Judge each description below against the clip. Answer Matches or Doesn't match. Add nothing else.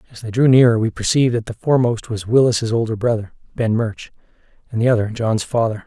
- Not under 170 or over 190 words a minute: Doesn't match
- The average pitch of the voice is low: Matches